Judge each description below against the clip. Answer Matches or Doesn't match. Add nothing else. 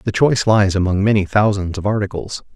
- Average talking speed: Matches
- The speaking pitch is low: Matches